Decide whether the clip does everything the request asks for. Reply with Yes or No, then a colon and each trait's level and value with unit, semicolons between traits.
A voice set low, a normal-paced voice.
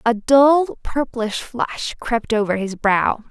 No: high, 235 Hz; average, 145 wpm